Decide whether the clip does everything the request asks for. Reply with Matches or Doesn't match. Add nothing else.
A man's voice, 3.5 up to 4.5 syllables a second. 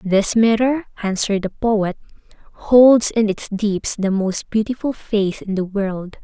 Doesn't match